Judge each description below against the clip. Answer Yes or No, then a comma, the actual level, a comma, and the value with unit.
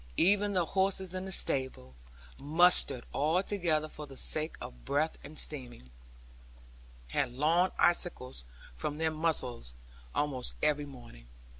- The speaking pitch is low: No, medium, 150 Hz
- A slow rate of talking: Yes, slow, 130 wpm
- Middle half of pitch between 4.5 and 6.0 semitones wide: Yes, average, 5.2 semitones